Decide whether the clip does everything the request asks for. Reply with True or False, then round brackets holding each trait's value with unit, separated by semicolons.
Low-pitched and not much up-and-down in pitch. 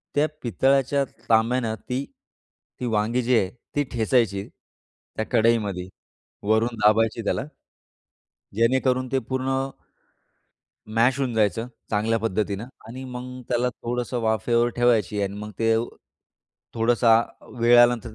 True (115 Hz; 2.2 semitones)